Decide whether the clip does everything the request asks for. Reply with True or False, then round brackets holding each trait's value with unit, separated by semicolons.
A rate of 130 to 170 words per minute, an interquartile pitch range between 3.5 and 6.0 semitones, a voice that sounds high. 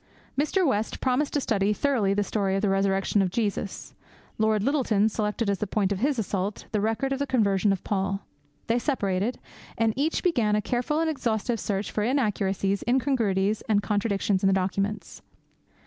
False (180 wpm; 3.9 semitones; 210 Hz)